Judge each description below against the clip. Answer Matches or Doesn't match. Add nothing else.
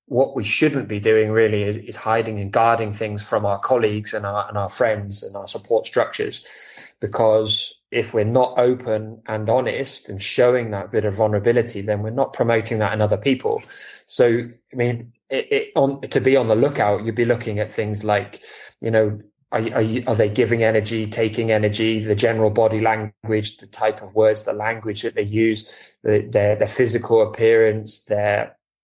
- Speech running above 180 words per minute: Matches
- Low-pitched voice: Matches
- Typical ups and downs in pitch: Doesn't match